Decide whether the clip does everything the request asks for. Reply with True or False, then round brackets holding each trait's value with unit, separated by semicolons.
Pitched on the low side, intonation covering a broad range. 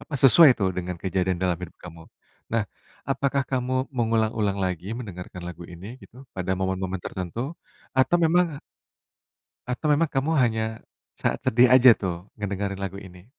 True (105 Hz; 5.9 semitones)